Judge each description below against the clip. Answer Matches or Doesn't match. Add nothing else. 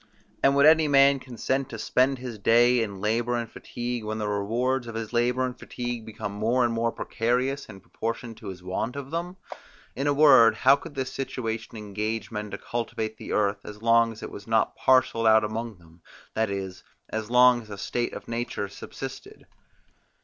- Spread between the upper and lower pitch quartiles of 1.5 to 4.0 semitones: Matches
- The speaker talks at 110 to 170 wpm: Doesn't match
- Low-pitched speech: Matches